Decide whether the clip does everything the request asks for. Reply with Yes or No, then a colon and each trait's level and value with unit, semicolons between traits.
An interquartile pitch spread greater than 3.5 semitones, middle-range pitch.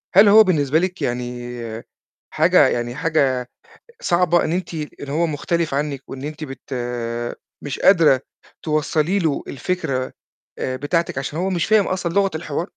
Yes: average, 4.3 semitones; medium, 155 Hz